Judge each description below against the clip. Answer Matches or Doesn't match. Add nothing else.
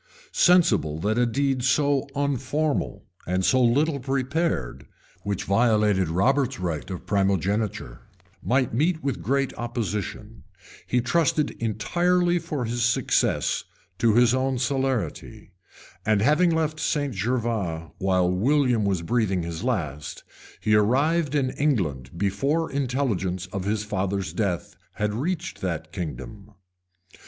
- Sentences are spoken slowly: Matches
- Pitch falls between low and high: Doesn't match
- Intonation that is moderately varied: Doesn't match